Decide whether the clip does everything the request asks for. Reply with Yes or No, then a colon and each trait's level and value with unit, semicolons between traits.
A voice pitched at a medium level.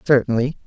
No: low, 125 Hz